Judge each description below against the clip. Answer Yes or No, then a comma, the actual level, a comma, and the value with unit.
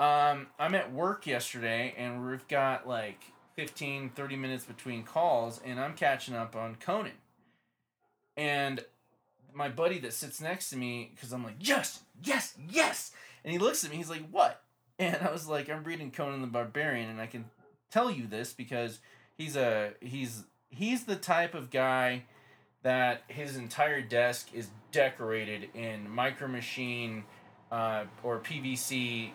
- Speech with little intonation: No, average, 3.7 semitones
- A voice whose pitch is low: Yes, low, 130 Hz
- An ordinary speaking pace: Yes, average, 160 wpm